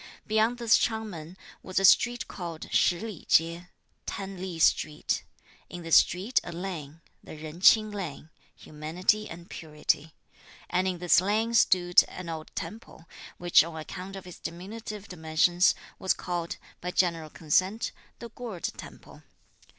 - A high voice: No, medium, 180 Hz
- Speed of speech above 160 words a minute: No, average, 150 wpm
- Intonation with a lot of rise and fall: No, average, 3.6 semitones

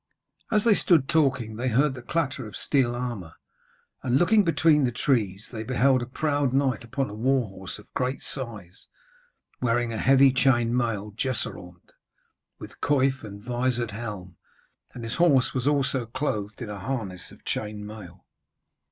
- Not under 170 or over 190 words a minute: No, average, 160 wpm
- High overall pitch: No, low, 125 Hz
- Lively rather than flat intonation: No, average, 4.0 semitones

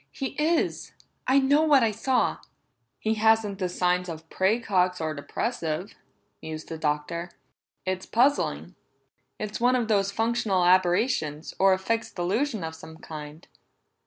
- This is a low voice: No, high, 195 Hz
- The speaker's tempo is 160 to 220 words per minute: No, average, 140 wpm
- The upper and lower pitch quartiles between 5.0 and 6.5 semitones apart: Yes, wide, 5.5 semitones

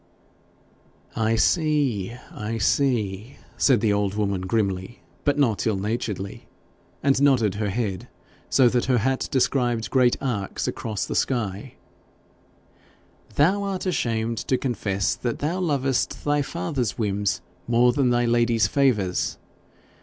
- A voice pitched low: Yes, low, 120 Hz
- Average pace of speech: No, slow, 130 wpm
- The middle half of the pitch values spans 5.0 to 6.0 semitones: No, average, 4.6 semitones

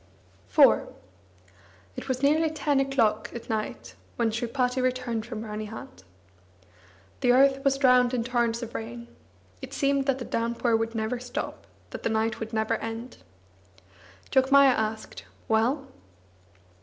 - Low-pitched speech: No, high, 240 Hz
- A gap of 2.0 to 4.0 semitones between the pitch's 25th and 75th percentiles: Yes, average, 3.0 semitones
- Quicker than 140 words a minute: No, slow, 135 wpm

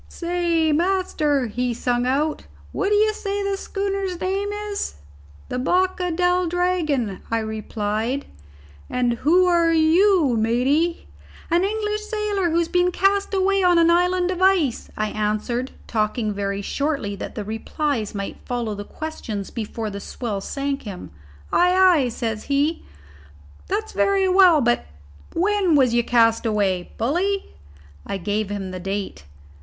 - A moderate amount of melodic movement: No, wide, 8.5 semitones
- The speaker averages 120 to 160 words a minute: Yes, average, 145 wpm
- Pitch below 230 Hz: No, very high, 305 Hz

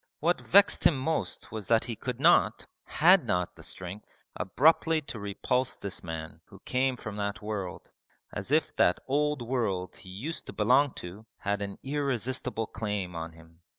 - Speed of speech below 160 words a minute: No, average, 170 wpm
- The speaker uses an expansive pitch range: Yes, wide, 6.0 semitones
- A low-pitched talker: Yes, low, 110 Hz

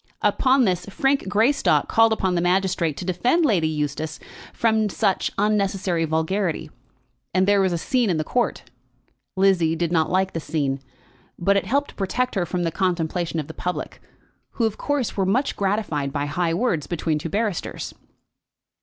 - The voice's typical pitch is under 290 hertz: Yes, medium, 185 Hz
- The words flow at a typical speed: Yes, average, 170 wpm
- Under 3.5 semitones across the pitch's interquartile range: No, average, 4.5 semitones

